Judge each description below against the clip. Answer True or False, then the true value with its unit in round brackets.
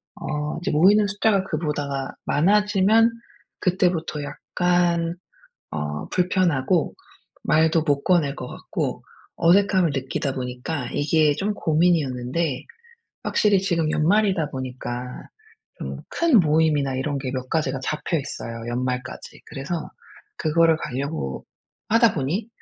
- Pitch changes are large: False (5.0 semitones)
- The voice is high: False (155 Hz)